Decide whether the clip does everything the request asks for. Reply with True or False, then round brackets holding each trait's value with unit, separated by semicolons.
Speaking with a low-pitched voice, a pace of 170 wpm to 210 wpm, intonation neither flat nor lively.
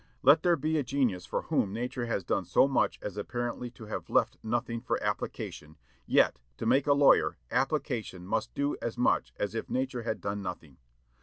True (120 Hz; 190 wpm; 4.6 semitones)